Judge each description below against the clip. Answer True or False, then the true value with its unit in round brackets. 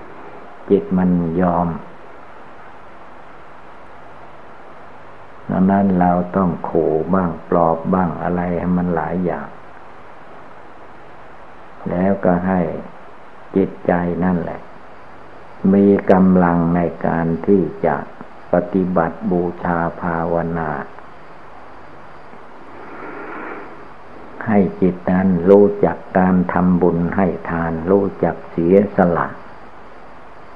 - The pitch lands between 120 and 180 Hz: False (90 Hz)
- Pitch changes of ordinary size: False (1.8 semitones)